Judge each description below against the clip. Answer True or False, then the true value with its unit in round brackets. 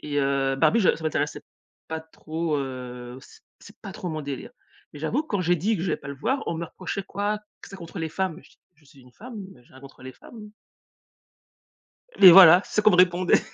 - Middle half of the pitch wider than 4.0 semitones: True (5.6 semitones)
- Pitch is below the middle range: False (165 Hz)